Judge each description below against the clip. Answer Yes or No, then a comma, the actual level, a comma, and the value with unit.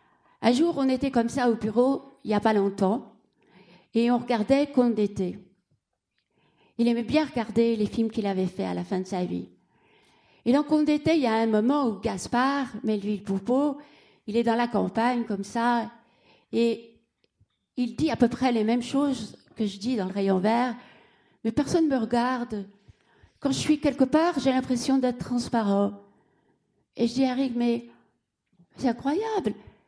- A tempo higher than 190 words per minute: No, average, 180 wpm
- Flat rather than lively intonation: No, average, 3.8 semitones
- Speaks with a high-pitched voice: Yes, high, 235 Hz